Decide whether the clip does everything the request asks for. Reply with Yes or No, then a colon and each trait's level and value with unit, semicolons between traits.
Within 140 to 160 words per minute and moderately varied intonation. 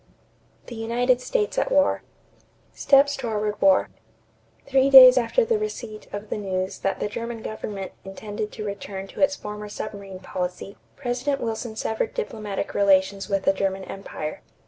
Yes: average, 150 wpm; average, 4.4 semitones